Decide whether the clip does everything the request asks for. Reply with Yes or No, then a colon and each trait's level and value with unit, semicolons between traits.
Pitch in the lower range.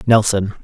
Yes: low, 105 Hz